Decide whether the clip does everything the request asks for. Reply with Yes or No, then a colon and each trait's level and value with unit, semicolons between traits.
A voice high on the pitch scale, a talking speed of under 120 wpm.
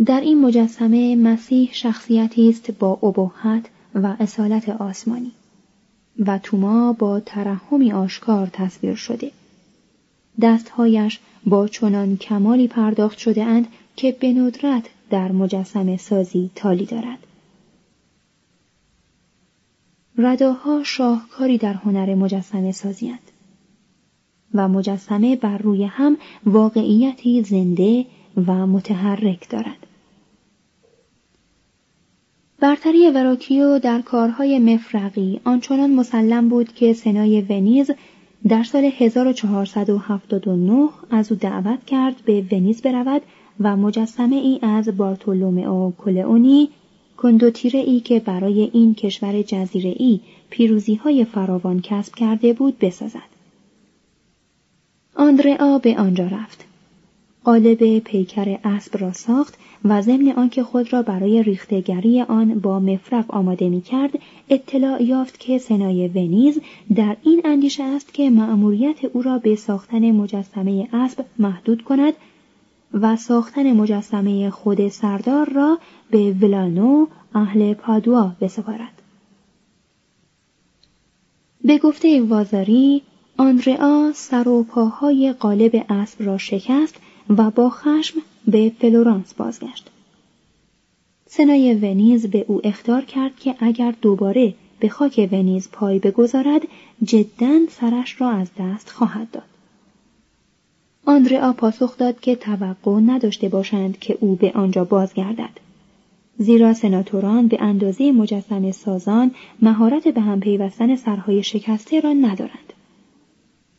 Yes: high, 220 Hz; average, 110 wpm